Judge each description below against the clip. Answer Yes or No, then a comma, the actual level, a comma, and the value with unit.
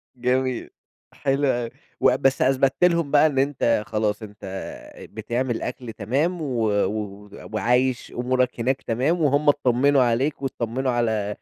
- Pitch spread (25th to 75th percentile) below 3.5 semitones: Yes, average, 3.1 semitones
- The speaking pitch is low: Yes, low, 125 Hz